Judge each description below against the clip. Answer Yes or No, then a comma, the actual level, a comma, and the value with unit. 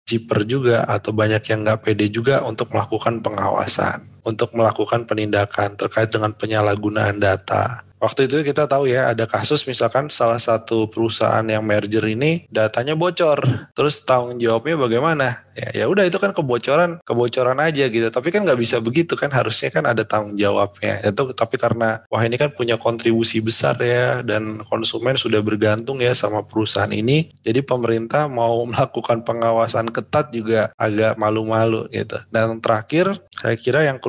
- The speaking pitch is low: Yes, low, 115 Hz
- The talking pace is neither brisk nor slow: No, fast, 160 wpm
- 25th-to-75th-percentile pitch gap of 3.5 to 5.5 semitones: No, narrow, 2.6 semitones